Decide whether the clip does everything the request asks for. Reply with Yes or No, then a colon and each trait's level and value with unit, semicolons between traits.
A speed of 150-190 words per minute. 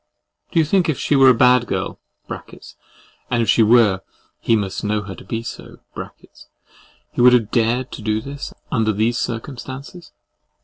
Yes: average, 170 wpm